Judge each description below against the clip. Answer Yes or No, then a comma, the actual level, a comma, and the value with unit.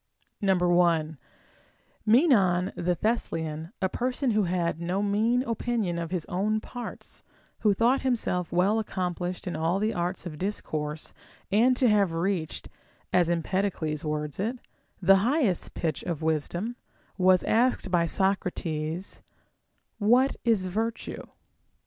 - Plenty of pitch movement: No, average, 4.3 semitones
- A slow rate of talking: Yes, slow, 130 wpm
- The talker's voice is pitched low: No, medium, 185 Hz